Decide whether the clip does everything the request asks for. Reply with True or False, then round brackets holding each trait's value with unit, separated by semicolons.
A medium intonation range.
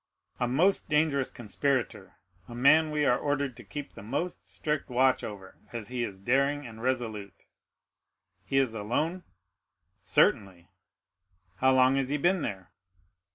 True (4.4 semitones)